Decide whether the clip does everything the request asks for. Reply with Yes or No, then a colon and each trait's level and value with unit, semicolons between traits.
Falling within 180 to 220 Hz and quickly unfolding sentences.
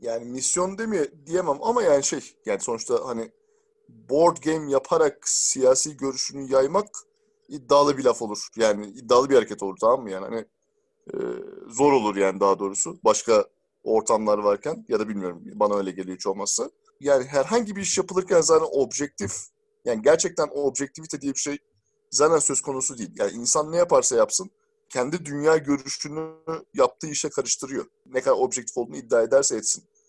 No: medium, 160 Hz; fast, 160 wpm